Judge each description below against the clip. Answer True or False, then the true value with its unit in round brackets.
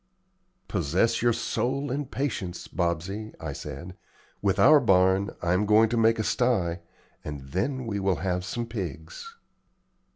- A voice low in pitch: True (100 Hz)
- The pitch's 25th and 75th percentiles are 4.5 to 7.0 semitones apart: True (5.0 semitones)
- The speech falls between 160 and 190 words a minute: False (150 wpm)